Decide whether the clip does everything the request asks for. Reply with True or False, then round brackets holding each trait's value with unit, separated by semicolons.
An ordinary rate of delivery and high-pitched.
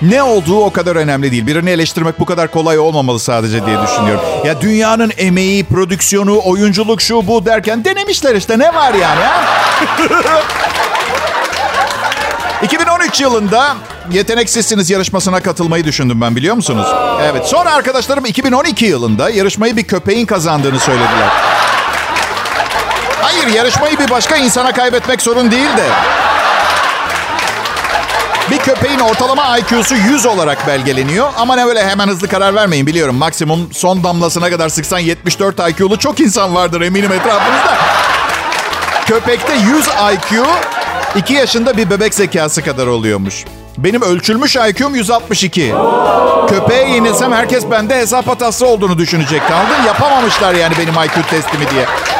True (130 wpm; 200 Hz)